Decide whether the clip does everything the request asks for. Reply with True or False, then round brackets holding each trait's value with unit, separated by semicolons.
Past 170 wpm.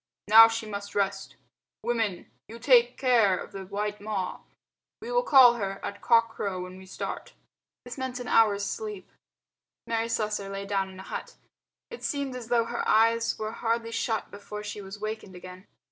True (180 wpm)